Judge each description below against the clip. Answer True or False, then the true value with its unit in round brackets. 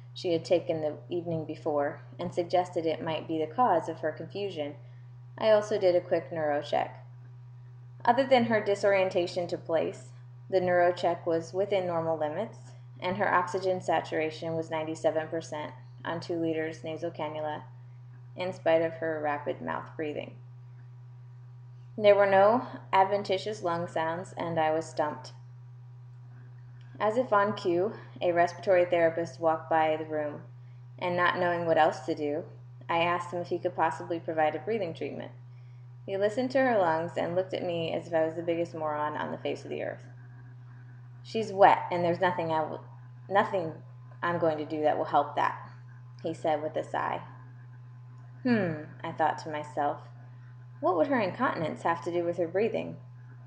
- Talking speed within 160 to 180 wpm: True (170 wpm)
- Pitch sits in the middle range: True (160 Hz)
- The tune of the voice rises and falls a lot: True (6.0 semitones)